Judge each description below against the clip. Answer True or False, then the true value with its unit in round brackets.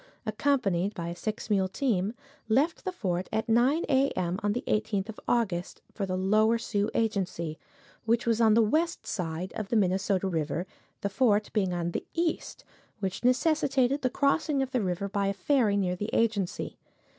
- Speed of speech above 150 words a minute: True (180 wpm)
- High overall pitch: True (210 Hz)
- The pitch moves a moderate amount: True (4.5 semitones)